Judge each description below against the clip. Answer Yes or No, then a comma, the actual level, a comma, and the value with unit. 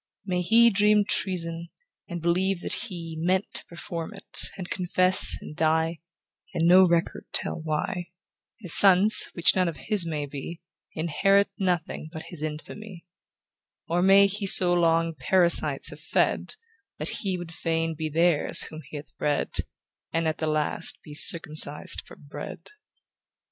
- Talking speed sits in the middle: Yes, average, 155 wpm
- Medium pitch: Yes, medium, 170 Hz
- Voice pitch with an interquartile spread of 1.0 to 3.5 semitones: Yes, average, 2.7 semitones